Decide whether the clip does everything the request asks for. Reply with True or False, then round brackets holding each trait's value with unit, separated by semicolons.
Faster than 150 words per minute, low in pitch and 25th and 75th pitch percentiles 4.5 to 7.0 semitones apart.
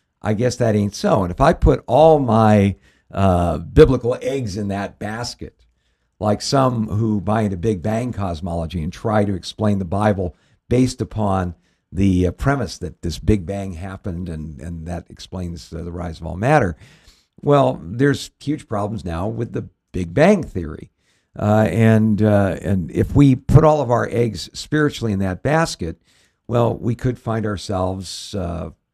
True (170 wpm; 105 Hz; 4.9 semitones)